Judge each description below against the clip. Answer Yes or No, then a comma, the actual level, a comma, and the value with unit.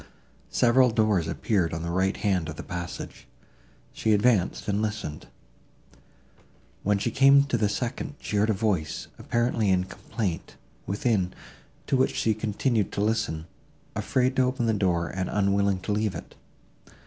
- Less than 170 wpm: Yes, average, 155 wpm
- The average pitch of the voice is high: No, low, 105 Hz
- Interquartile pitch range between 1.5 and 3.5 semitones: No, average, 3.9 semitones